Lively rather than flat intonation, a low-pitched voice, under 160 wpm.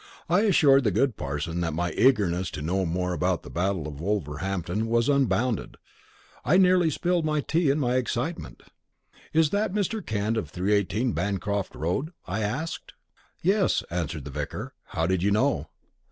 No: wide, 8.4 semitones; low, 105 Hz; average, 165 wpm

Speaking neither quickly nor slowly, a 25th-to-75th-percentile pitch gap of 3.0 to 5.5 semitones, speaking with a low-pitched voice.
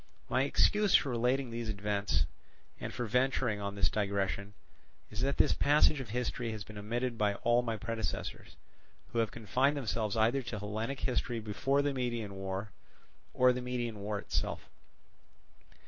Yes: average, 160 wpm; average, 3.4 semitones; low, 115 Hz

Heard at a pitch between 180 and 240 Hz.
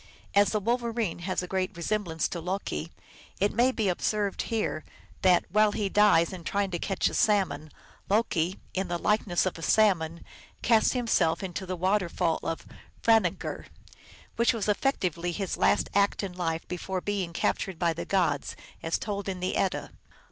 Yes: high, 190 Hz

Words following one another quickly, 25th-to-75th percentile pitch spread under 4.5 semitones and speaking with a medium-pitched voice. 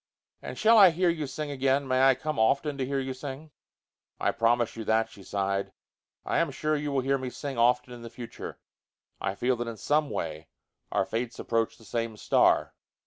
No: fast, 210 wpm; average, 3.8 semitones; low, 130 Hz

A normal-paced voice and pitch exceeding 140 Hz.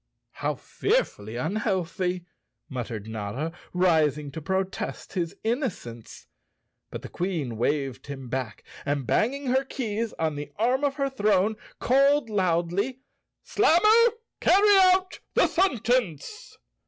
No: slow, 115 wpm; high, 190 Hz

